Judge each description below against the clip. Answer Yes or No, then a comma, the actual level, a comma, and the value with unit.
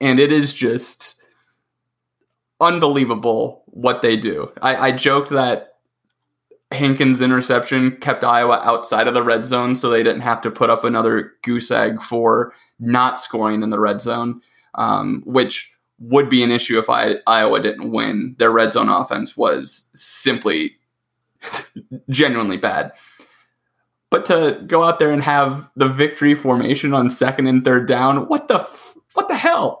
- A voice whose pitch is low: Yes, low, 130 Hz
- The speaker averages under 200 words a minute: Yes, average, 155 wpm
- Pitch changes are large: No, average, 3.0 semitones